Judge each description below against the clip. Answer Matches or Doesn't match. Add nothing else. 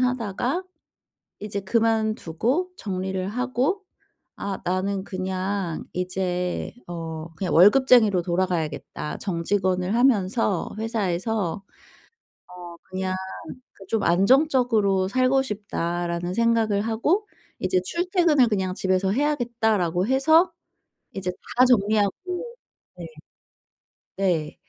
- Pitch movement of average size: Matches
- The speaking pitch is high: Matches